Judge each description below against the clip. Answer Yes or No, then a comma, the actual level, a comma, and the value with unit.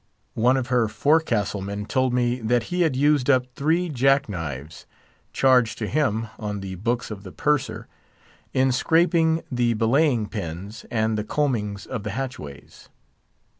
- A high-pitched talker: No, low, 120 Hz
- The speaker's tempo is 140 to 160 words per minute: Yes, average, 155 wpm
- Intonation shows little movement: No, average, 4.5 semitones